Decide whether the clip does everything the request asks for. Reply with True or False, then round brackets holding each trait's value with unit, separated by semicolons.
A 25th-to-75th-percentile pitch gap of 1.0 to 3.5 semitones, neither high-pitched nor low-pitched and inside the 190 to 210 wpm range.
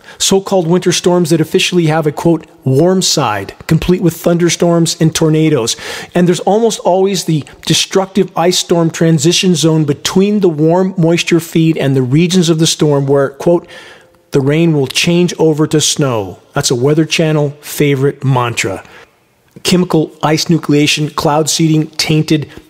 False (2.8 semitones; 160 Hz; 155 wpm)